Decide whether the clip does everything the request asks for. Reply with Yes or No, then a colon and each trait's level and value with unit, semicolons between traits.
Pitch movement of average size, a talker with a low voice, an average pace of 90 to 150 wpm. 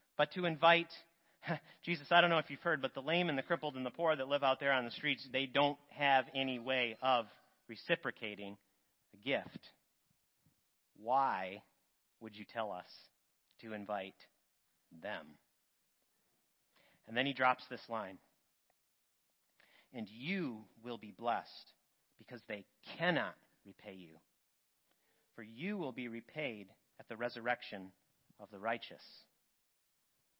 Yes: average, 4.6 semitones; low, 130 Hz; average, 140 wpm